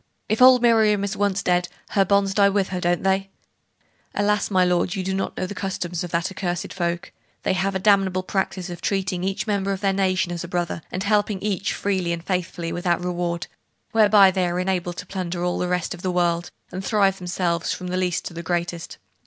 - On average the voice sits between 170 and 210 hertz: Yes, medium, 185 Hz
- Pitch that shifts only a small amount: Yes, narrow, 2.0 semitones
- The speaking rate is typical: No, fast, 220 wpm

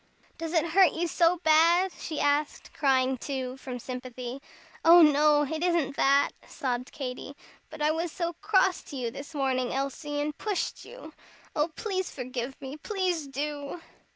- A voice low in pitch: No, very high, 295 Hz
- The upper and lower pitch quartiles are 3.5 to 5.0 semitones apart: Yes, average, 3.9 semitones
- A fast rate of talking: No, average, 160 wpm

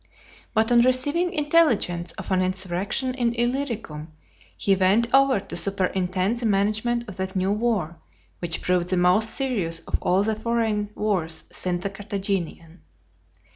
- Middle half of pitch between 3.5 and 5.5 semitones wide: Yes, average, 4.5 semitones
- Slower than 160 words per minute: Yes, average, 145 wpm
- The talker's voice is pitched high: Yes, high, 200 Hz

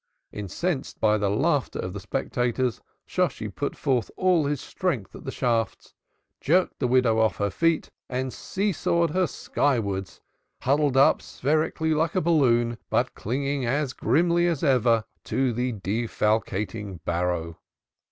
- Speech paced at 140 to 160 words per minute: Yes, average, 145 wpm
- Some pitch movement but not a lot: No, wide, 5.7 semitones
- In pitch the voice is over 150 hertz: No, low, 125 Hz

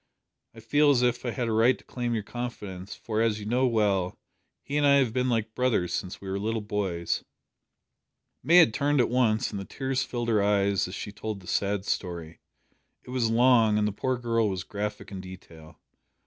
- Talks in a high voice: No, low, 110 Hz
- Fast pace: Yes, fast, 210 wpm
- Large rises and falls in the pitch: No, average, 3.7 semitones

